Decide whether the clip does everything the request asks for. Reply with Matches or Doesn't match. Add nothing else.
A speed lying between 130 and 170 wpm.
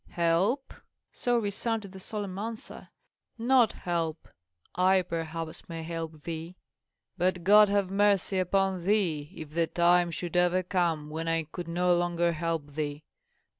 Matches